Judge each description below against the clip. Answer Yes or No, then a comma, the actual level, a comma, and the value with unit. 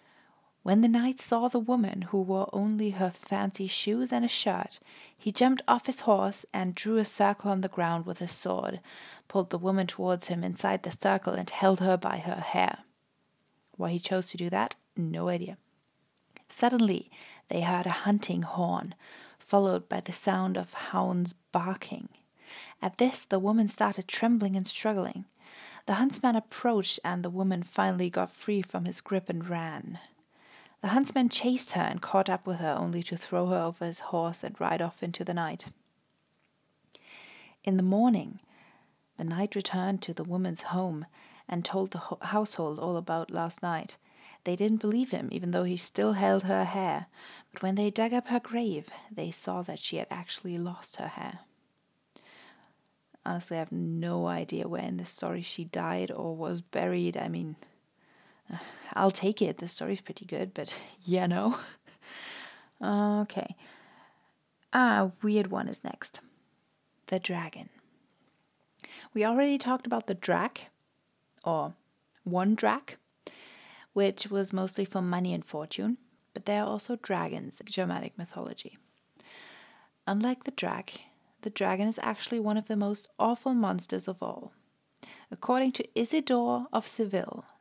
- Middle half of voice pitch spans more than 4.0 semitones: No, average, 3.7 semitones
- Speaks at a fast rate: No, average, 160 wpm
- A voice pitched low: No, high, 195 Hz